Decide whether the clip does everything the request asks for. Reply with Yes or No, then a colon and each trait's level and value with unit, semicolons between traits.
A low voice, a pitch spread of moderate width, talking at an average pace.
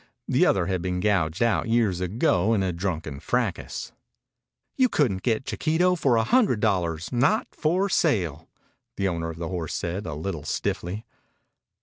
No: very low, 95 Hz; wide, 5.8 semitones; average, 160 wpm